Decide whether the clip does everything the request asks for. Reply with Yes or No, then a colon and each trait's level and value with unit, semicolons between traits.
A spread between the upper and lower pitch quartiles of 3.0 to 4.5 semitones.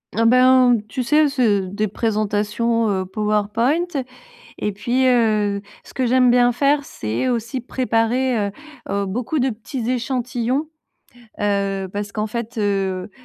Yes: average, 3.5 semitones